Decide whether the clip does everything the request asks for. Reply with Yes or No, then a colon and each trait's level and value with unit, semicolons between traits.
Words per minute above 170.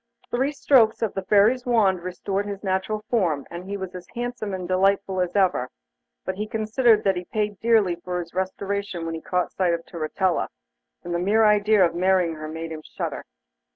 Yes: average, 195 wpm